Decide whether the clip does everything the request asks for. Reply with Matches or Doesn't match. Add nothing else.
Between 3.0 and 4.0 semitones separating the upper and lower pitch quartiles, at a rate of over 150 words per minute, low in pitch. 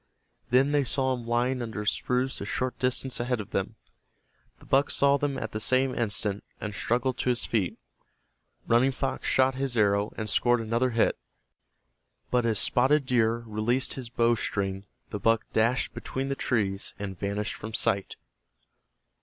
Matches